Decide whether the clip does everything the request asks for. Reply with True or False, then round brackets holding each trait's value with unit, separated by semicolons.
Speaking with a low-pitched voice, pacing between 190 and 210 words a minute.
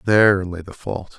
True (95 Hz; 205 wpm)